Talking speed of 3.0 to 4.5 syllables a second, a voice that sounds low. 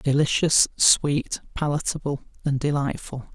No: 4.2 syllables/s; medium, 145 Hz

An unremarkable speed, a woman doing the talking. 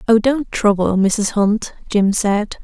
Yes: average, 160 wpm; female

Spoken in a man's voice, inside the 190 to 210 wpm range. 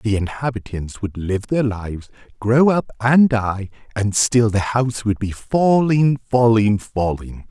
No: male; average, 150 wpm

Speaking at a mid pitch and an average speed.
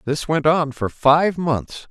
Yes: medium, 150 Hz; average, 190 wpm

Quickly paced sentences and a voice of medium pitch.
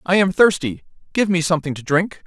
Yes: fast, 210 wpm; medium, 175 Hz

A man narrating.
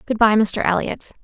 No: female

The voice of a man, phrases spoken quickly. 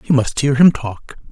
Yes: male; fast, 230 wpm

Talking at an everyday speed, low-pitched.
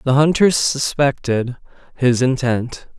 No: slow, 100 wpm; low, 130 Hz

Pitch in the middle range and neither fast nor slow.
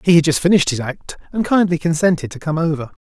No: medium, 160 Hz; fast, 240 wpm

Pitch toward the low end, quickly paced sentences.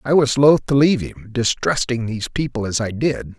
Yes: low, 125 Hz; fast, 215 wpm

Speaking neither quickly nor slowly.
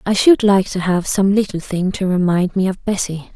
No: fast, 235 wpm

